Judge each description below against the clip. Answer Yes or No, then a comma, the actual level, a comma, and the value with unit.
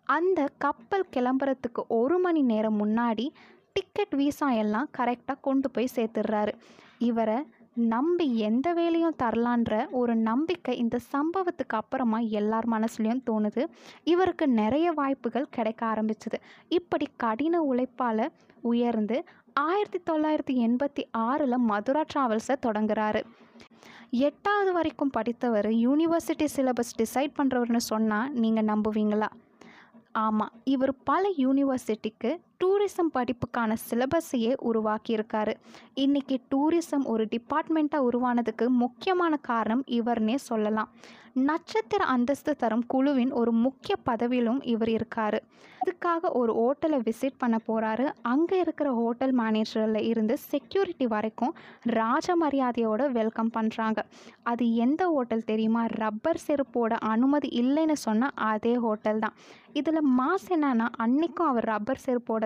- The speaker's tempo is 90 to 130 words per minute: Yes, average, 110 wpm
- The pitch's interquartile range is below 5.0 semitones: Yes, average, 4.4 semitones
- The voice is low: No, high, 245 Hz